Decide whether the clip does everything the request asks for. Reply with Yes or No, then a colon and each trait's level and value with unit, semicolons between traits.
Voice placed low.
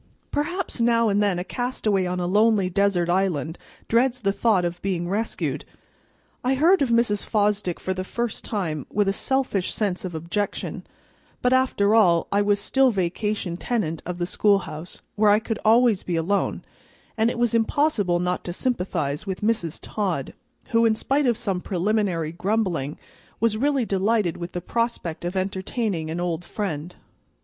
No: high, 200 Hz